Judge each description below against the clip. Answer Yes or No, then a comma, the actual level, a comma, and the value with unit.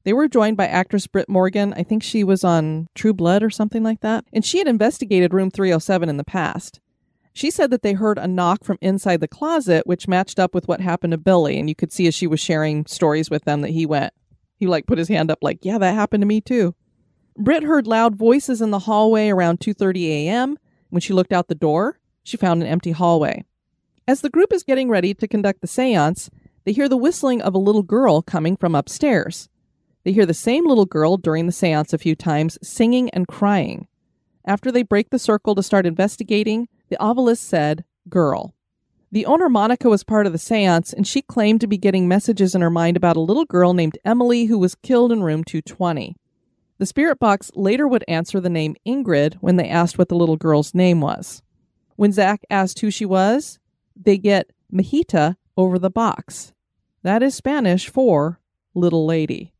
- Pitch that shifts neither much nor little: Yes, average, 4.5 semitones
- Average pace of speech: No, fast, 210 wpm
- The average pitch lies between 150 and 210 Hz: Yes, high, 190 Hz